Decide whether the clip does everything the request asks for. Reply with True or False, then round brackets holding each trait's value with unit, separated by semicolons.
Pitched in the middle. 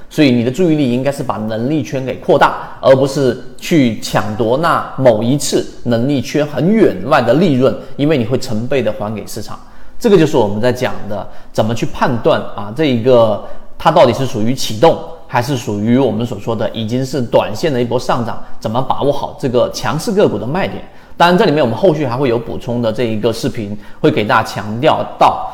False (125 Hz)